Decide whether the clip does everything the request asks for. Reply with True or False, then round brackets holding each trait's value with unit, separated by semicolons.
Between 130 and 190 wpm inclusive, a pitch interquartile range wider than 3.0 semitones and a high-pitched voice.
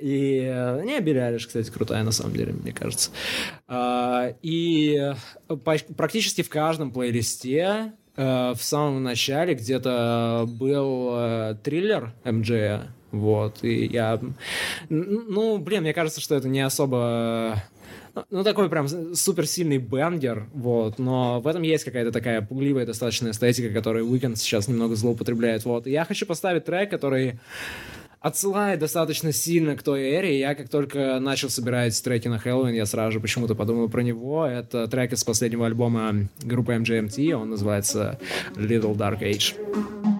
False (145 wpm; 4.8 semitones; 125 Hz)